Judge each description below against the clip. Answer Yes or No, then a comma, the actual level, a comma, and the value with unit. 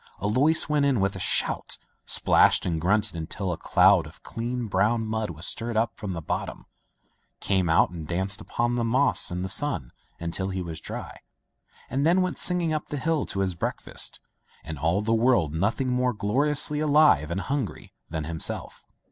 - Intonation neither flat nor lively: No, wide, 7.0 semitones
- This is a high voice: No, low, 110 Hz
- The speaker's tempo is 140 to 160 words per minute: No, average, 180 wpm